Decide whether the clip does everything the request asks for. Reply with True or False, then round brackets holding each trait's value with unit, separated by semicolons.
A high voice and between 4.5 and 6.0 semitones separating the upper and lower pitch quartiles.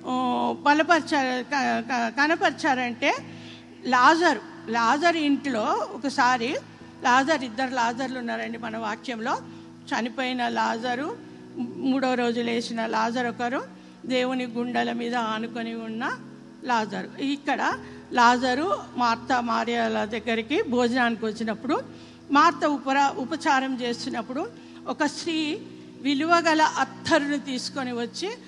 False (255 Hz; 3.5 semitones)